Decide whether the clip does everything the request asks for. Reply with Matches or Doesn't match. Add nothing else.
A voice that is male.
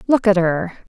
Doesn't match